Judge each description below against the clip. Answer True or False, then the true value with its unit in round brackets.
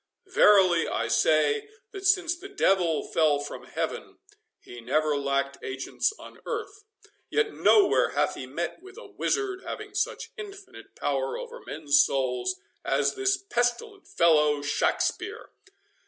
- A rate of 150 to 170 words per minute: False (135 wpm)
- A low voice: False (240 Hz)